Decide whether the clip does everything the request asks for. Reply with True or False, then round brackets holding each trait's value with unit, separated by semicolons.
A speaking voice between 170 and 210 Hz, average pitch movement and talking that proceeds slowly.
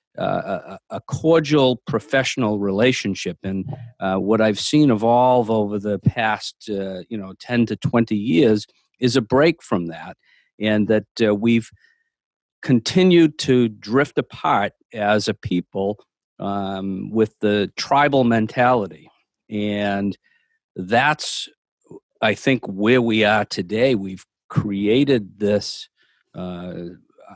False (110 Hz; 4.0 semitones; 120 wpm)